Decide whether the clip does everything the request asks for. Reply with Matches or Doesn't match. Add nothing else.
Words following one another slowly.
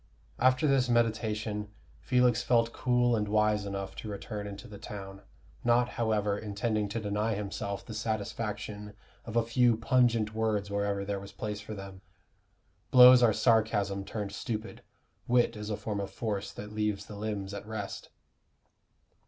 Doesn't match